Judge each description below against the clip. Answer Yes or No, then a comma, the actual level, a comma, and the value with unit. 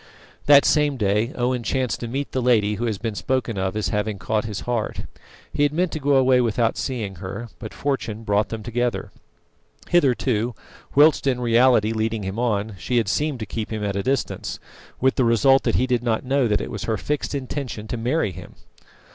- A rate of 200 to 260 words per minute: Yes, fast, 205 wpm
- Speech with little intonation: No, average, 3.7 semitones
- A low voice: Yes, low, 120 Hz